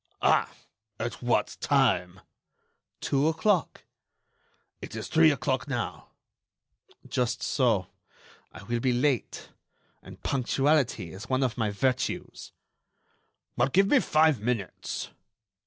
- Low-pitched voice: Yes, low, 130 Hz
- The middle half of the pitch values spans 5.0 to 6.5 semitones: No, average, 4.0 semitones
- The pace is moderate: No, slow, 110 wpm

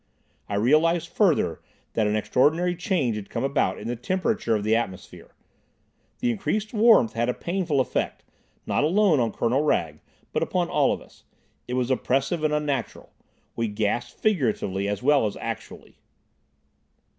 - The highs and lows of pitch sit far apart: Yes, wide, 7.3 semitones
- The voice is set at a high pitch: No, low, 135 Hz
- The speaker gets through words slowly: No, average, 155 wpm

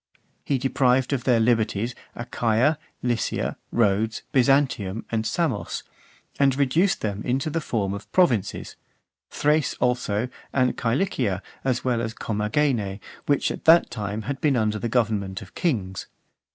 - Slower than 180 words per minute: Yes, average, 140 wpm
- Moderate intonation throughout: Yes, average, 4.2 semitones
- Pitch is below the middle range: Yes, low, 120 Hz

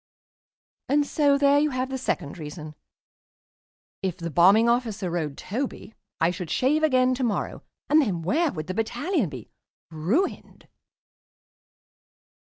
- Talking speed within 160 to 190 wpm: No, slow, 135 wpm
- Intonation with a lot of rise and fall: Yes, wide, 8.6 semitones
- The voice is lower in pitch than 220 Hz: No, high, 225 Hz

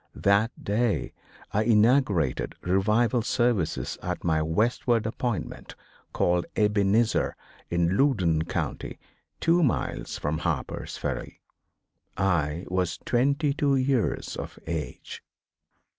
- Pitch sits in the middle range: No, low, 105 Hz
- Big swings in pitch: Yes, wide, 5.7 semitones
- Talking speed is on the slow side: Yes, slow, 100 wpm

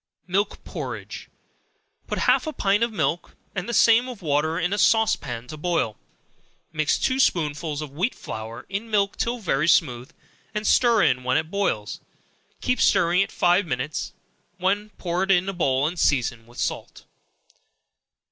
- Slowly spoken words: No, average, 165 wpm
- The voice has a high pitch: No, medium, 175 Hz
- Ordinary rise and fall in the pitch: No, wide, 6.1 semitones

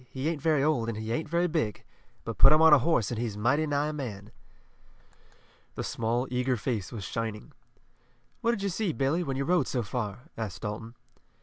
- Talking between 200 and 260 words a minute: Yes, fast, 205 wpm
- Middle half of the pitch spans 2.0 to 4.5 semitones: No, wide, 5.5 semitones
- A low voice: Yes, low, 130 Hz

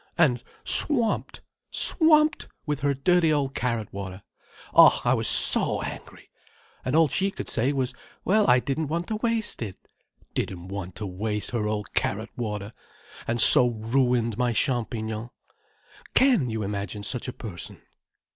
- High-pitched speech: No, low, 120 Hz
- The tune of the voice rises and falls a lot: Yes, wide, 6.3 semitones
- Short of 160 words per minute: Yes, average, 145 wpm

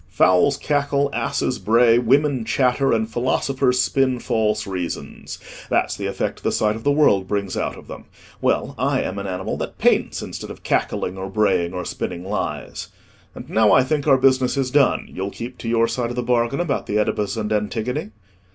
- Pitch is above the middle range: No, low, 115 Hz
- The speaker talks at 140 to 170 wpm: No, average, 190 wpm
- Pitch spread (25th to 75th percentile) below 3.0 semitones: No, average, 4.3 semitones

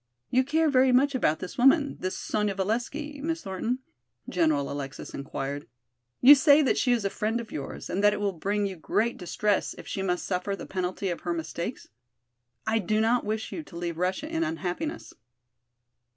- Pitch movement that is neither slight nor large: No, wide, 6.4 semitones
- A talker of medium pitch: No, high, 210 Hz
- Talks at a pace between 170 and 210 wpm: Yes, average, 190 wpm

